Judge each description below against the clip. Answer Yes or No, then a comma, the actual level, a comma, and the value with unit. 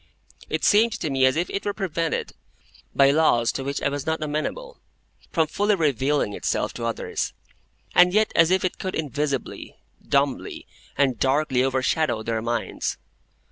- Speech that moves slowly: No, average, 160 wpm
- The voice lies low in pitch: No, medium, 150 Hz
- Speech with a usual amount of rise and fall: Yes, average, 5.0 semitones